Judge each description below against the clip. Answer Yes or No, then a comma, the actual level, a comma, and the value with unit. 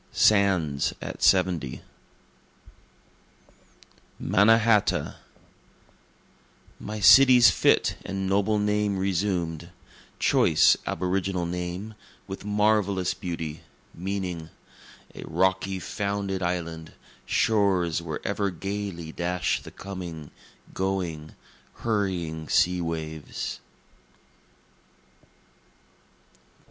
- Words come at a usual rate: No, slow, 75 wpm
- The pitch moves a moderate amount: Yes, average, 3.1 semitones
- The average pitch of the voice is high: No, very low, 95 Hz